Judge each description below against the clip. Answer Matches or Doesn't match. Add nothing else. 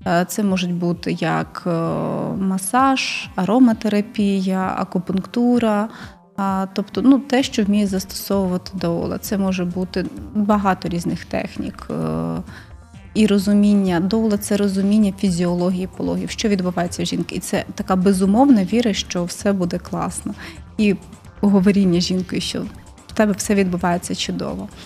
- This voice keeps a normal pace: Matches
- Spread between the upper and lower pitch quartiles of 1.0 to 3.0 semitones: Matches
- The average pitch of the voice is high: Matches